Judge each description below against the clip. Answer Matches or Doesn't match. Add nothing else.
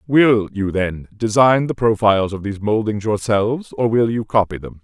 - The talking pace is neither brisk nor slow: Matches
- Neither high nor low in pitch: Doesn't match